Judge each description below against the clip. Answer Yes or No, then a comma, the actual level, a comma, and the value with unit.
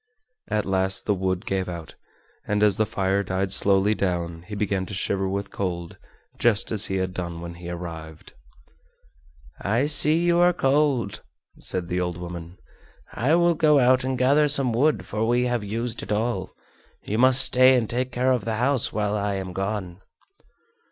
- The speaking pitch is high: No, low, 105 Hz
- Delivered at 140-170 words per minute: No, average, 180 wpm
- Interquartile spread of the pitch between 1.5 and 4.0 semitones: No, average, 5.1 semitones